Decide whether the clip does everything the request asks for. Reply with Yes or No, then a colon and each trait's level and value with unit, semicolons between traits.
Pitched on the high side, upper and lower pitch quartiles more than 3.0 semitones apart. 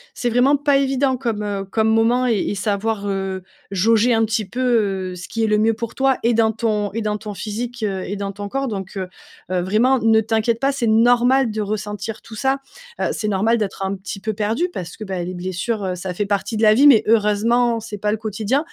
No: high, 220 Hz; average, 2.7 semitones